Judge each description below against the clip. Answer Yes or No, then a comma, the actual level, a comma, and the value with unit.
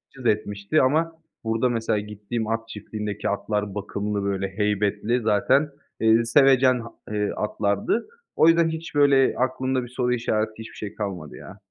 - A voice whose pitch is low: Yes, low, 110 Hz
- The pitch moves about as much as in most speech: Yes, average, 3.8 semitones